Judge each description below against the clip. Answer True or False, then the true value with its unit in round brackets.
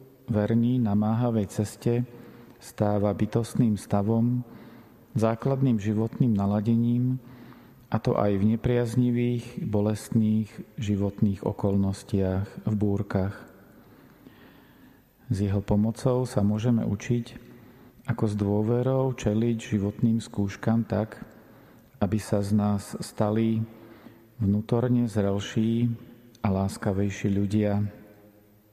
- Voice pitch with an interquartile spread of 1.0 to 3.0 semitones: True (2.5 semitones)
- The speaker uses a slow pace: True (90 wpm)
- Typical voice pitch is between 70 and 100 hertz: False (110 Hz)